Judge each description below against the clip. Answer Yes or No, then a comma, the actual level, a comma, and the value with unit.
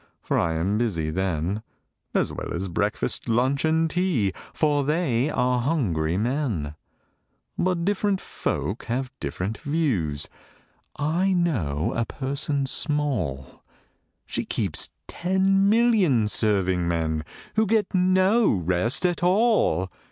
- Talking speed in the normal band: No, slow, 120 wpm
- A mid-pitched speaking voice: No, low, 130 Hz